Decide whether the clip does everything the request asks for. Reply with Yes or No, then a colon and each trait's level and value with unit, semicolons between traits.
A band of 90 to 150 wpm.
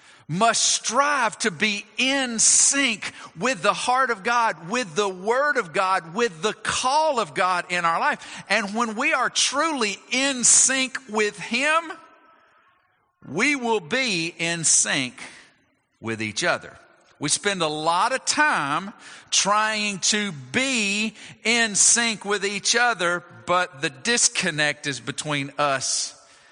Yes: average, 140 wpm